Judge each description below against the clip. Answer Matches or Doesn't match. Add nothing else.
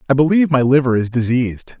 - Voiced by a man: Matches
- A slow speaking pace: Doesn't match